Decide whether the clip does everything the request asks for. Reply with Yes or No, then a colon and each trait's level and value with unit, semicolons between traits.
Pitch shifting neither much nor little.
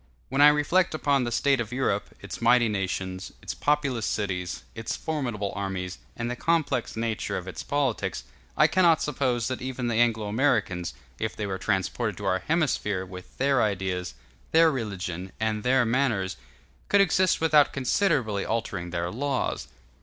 No: wide, 6.3 semitones